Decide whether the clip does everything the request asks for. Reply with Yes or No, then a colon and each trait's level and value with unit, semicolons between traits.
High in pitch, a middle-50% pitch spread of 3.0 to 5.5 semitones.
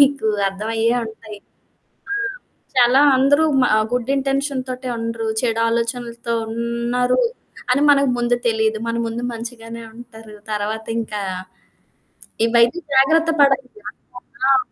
No: high, 235 Hz; narrow, 2.6 semitones